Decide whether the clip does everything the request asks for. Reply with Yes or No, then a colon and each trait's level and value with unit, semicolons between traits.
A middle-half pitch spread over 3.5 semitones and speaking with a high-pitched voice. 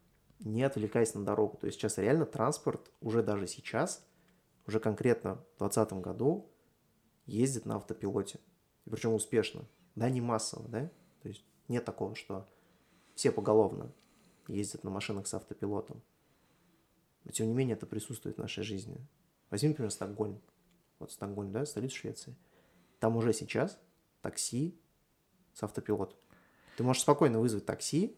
No: average, 3.9 semitones; low, 110 Hz